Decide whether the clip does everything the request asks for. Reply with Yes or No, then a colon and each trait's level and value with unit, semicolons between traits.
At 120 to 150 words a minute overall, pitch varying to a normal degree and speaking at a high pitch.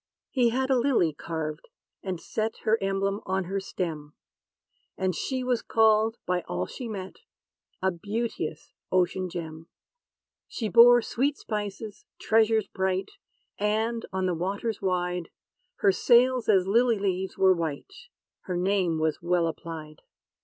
Yes: average, 140 wpm; average, 4.0 semitones; high, 195 Hz